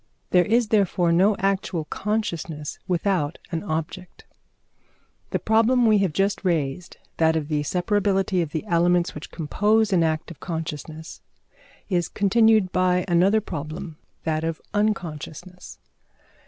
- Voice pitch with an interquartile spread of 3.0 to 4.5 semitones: Yes, average, 3.9 semitones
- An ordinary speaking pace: No, slow, 130 wpm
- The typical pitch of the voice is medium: Yes, medium, 180 Hz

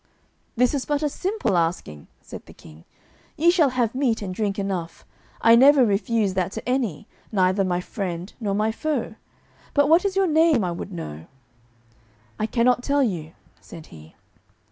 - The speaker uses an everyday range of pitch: No, wide, 7.2 semitones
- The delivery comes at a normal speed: Yes, average, 170 wpm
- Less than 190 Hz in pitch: No, high, 220 Hz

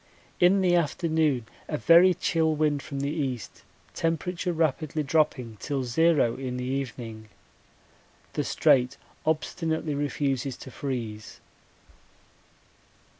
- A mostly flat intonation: No, average, 4.1 semitones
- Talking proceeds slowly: Yes, slow, 110 wpm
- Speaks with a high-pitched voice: No, medium, 145 Hz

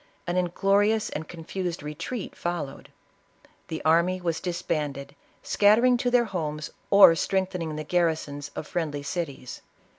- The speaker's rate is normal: No, slow, 130 wpm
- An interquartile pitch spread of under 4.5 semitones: Yes, average, 3.9 semitones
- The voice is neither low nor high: Yes, medium, 170 Hz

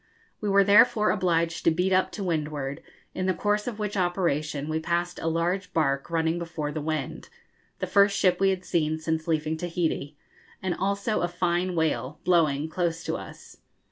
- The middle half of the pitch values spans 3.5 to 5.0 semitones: No, average, 3.0 semitones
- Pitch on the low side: No, medium, 170 Hz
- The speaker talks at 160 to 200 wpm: Yes, average, 180 wpm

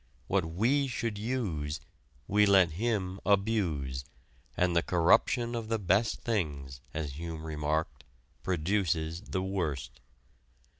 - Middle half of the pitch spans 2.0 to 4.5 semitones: No, average, 5.1 semitones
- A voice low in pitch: Yes, very low, 90 Hz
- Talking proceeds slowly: Yes, slow, 115 wpm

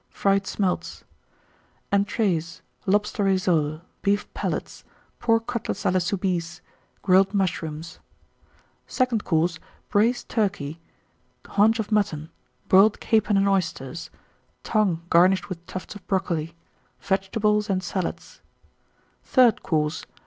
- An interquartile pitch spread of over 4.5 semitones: No, average, 3.6 semitones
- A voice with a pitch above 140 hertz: Yes, high, 190 Hz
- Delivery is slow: Yes, slow, 105 wpm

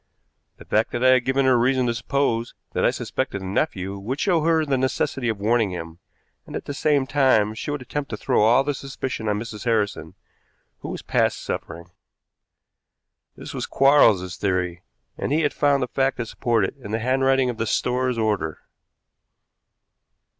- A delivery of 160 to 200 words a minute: Yes, average, 190 wpm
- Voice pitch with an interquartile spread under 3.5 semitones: No, average, 4.3 semitones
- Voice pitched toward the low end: Yes, low, 120 Hz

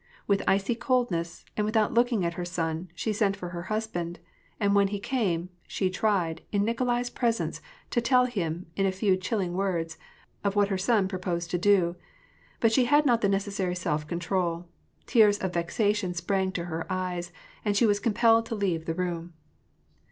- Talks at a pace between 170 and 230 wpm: Yes, average, 185 wpm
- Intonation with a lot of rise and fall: No, average, 3.7 semitones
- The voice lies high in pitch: Yes, high, 195 Hz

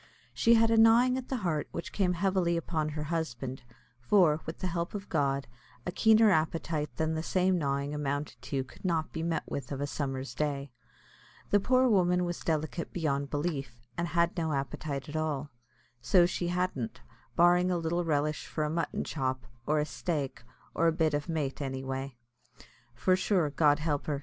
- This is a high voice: No, medium, 160 Hz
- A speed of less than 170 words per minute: No, average, 185 wpm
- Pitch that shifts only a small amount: No, average, 3.7 semitones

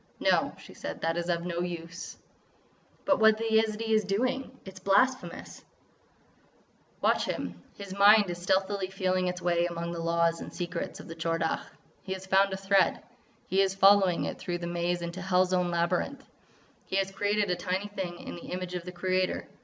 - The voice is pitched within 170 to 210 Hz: Yes, medium, 185 Hz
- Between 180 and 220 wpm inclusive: Yes, average, 190 wpm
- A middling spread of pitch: No, narrow, 2.3 semitones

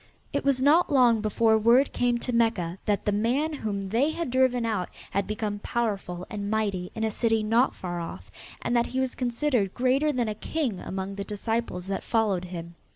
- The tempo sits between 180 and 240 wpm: Yes, average, 200 wpm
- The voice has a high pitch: Yes, high, 225 Hz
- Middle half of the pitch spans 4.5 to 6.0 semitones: No, average, 3.9 semitones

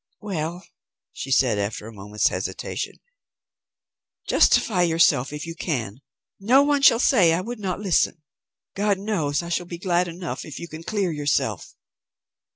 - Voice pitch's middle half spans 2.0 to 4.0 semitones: No, average, 5.2 semitones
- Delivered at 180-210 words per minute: No, average, 155 wpm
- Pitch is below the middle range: No, medium, 170 Hz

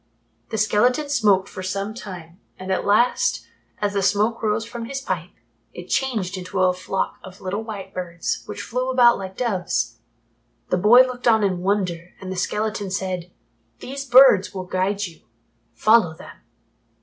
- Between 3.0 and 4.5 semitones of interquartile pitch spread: Yes, average, 3.6 semitones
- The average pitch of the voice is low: No, high, 200 Hz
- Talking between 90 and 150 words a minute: No, average, 165 wpm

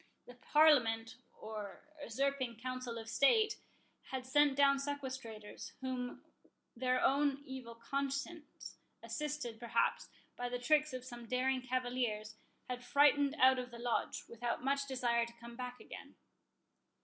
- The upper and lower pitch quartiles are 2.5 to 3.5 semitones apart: Yes, average, 2.8 semitones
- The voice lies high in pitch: Yes, very high, 255 Hz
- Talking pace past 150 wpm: No, slow, 135 wpm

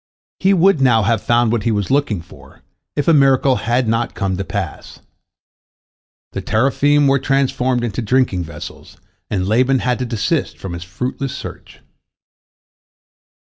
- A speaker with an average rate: Yes, average, 150 wpm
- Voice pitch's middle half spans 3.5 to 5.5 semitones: Yes, average, 4.4 semitones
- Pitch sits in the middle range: No, low, 120 Hz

